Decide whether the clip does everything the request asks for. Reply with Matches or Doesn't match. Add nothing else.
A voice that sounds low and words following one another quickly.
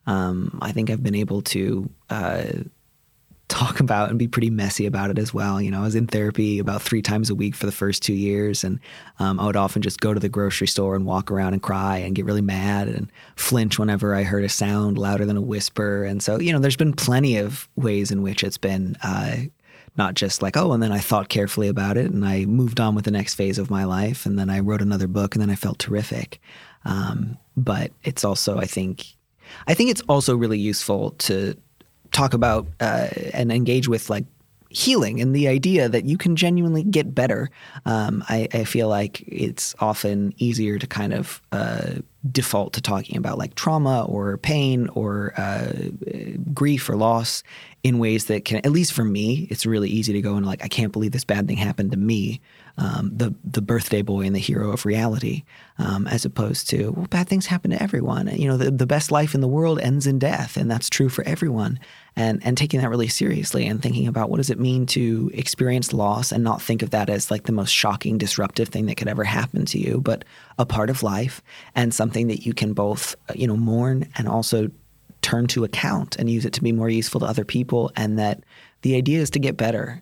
Matches